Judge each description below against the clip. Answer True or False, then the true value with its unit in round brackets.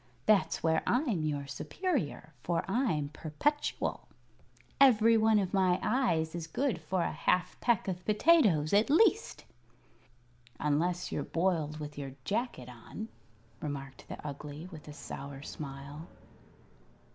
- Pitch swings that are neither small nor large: False (6.7 semitones)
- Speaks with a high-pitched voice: False (170 Hz)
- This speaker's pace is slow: True (130 wpm)